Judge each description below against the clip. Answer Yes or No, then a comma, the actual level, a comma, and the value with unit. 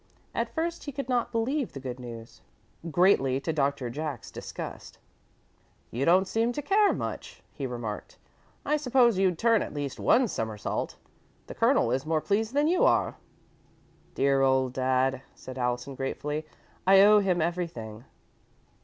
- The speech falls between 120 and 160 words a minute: Yes, average, 155 wpm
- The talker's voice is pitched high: No, medium, 155 Hz